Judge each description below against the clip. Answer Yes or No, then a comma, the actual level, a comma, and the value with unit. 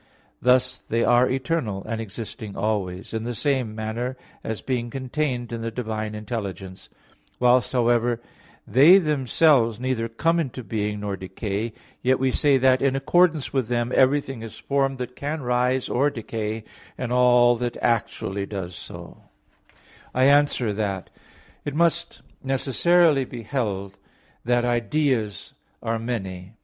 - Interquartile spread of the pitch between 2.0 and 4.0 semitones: Yes, average, 3.4 semitones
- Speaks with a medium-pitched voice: No, low, 120 Hz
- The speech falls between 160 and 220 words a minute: No, average, 140 wpm